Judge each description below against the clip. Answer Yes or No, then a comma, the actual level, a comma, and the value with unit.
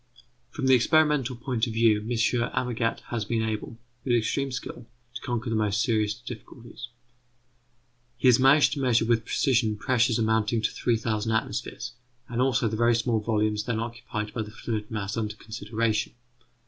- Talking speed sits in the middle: Yes, average, 165 wpm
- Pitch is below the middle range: Yes, low, 115 Hz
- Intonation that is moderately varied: No, narrow, 2.0 semitones